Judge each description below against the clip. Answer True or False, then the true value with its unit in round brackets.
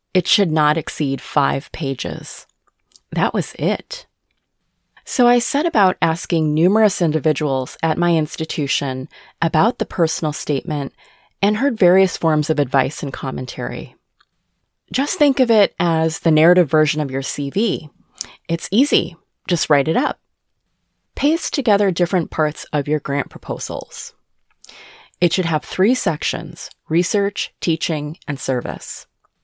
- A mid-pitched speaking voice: True (165 Hz)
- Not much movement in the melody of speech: False (4.5 semitones)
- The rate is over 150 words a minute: False (135 wpm)